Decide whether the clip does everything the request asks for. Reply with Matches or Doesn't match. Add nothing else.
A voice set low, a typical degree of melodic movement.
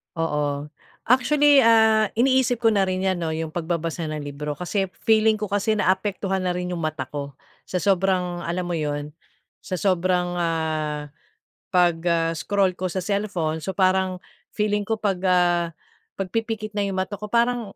Doesn't match